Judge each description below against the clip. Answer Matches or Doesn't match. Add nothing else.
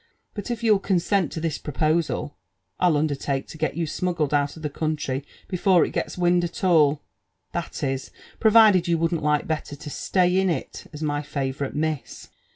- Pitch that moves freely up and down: Doesn't match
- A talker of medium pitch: Matches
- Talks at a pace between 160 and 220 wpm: Matches